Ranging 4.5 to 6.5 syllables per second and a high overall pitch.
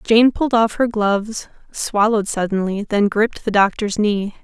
Yes: 5.0 syllables/s; high, 210 Hz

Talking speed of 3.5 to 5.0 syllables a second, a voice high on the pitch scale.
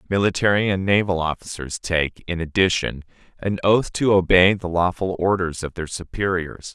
No: 4.9 syllables/s; very low, 90 Hz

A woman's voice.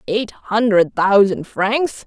Yes: female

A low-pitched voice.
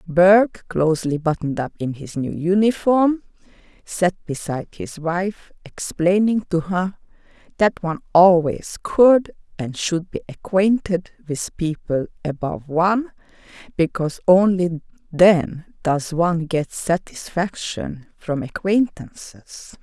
No: medium, 175 Hz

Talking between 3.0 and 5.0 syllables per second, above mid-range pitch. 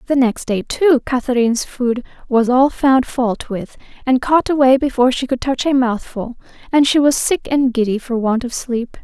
Yes: 4.8 syllables/s; very high, 255 Hz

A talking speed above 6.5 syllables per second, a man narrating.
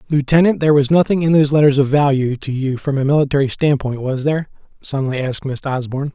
Yes: 6.8 syllables/s; male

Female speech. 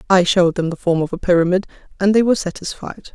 Yes: female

